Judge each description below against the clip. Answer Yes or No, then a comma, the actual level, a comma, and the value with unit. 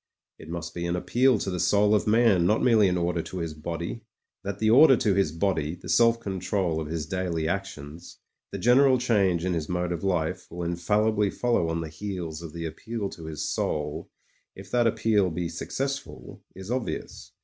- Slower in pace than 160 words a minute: No, fast, 205 wpm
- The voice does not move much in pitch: No, average, 4.3 semitones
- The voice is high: No, very low, 90 Hz